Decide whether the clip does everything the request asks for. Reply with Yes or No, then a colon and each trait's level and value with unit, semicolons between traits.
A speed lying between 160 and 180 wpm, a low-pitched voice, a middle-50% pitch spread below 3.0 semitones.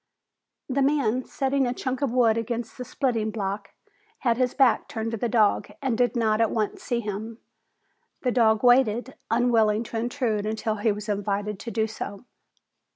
No: average, 175 wpm; high, 230 Hz; narrow, 2.5 semitones